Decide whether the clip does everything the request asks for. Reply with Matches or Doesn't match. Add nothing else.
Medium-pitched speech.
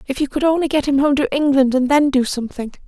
Doesn't match